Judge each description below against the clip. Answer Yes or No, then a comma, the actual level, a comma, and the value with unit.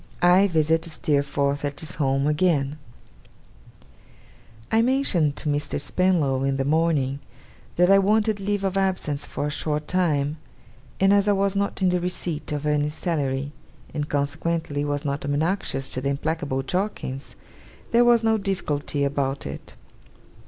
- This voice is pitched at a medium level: Yes, medium, 155 Hz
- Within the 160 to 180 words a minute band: No, average, 150 wpm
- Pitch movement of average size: Yes, average, 4.8 semitones